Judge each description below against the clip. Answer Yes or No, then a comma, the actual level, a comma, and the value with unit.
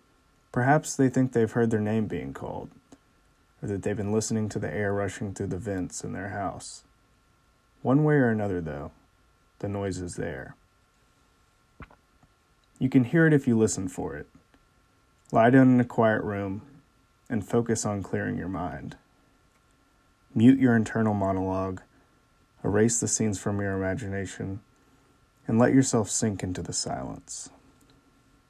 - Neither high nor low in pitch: No, low, 110 Hz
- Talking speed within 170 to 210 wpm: No, average, 150 wpm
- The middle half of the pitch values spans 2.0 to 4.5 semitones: No, average, 4.9 semitones